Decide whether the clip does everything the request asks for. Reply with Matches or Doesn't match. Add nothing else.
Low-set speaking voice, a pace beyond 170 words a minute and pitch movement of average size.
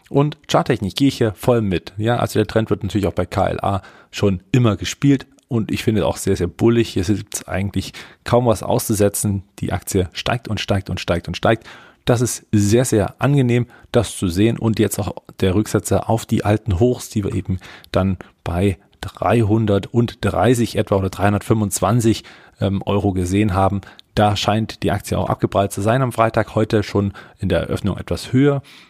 Matches